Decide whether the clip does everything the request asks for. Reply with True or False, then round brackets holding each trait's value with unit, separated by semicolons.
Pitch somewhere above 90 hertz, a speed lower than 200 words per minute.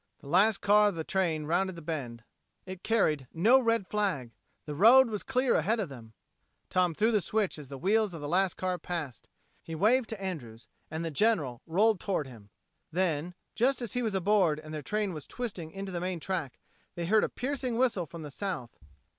False (185 Hz; 205 wpm)